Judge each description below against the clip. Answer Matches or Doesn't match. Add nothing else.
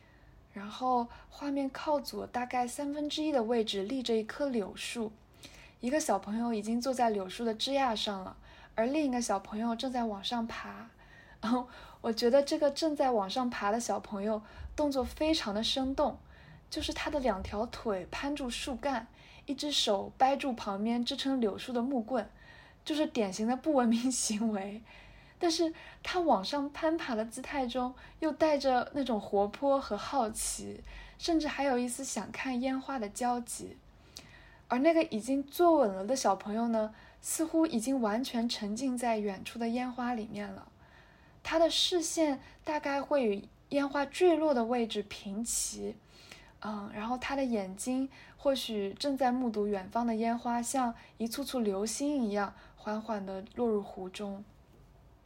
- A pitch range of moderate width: Matches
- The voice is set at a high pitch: Matches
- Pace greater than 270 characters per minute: Doesn't match